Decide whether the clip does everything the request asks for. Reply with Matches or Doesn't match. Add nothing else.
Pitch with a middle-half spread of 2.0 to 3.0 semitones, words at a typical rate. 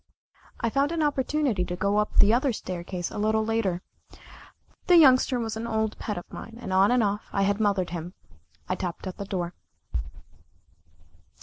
Doesn't match